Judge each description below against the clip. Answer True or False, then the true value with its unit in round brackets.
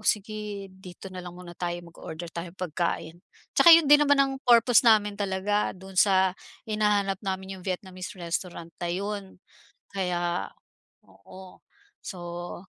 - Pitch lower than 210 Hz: True (190 Hz)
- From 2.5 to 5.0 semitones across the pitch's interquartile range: True (2.9 semitones)